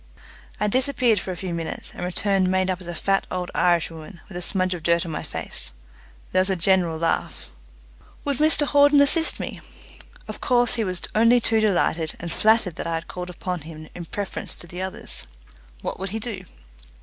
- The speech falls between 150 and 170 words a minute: No, fast, 205 wpm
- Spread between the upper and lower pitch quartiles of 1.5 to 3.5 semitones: No, average, 4.2 semitones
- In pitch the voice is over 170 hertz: Yes, medium, 185 Hz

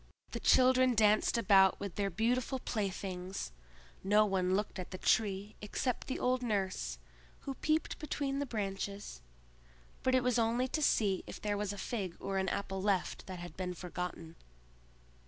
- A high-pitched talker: Yes, high, 205 Hz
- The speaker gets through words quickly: No, average, 165 wpm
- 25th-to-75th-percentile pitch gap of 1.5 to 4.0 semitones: No, average, 4.4 semitones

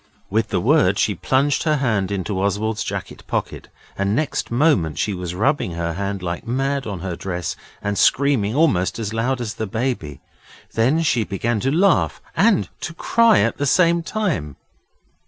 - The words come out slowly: No, average, 175 wpm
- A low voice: Yes, low, 110 Hz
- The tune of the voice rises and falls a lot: Yes, wide, 6.4 semitones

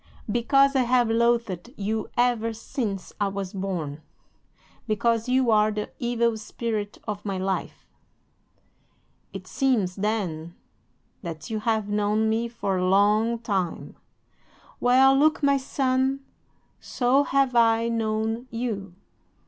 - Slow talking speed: Yes, slow, 125 wpm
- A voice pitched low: No, high, 225 Hz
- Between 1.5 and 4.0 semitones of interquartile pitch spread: Yes, average, 3.1 semitones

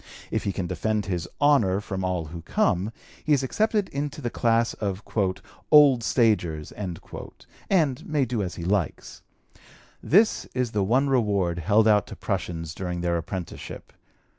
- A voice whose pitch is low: Yes, low, 105 Hz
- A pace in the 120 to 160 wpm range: Yes, average, 155 wpm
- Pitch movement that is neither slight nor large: No, wide, 6.4 semitones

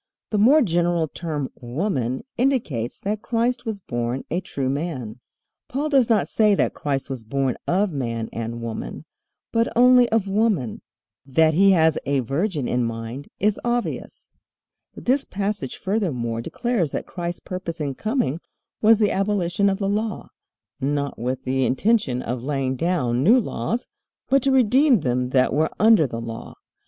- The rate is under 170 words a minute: Yes, average, 160 wpm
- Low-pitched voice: No, medium, 170 Hz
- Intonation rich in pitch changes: Yes, wide, 8.7 semitones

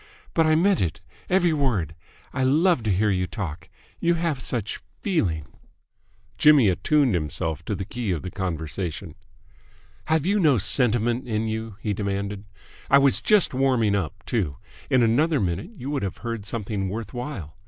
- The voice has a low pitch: Yes, low, 115 Hz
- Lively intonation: Yes, wide, 6.9 semitones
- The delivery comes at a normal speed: Yes, average, 165 wpm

